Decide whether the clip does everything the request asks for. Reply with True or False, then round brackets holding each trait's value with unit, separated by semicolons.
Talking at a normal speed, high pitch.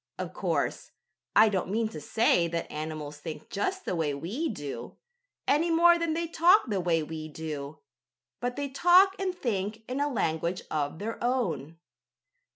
True (165 wpm; 200 Hz)